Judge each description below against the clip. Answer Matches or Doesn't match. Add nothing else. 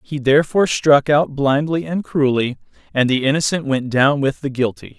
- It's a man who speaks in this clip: Matches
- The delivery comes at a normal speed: Matches